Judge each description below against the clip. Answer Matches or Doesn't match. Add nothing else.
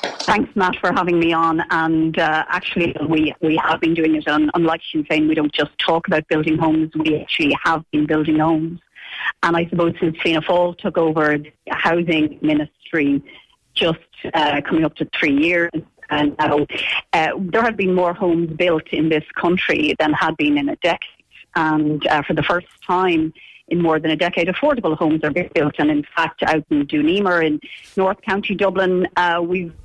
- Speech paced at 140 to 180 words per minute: Doesn't match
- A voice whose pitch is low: Doesn't match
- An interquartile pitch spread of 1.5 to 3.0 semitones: Matches